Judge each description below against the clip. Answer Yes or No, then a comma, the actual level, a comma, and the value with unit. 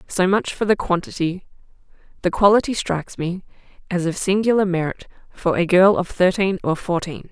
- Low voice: No, medium, 185 Hz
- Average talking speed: Yes, average, 165 wpm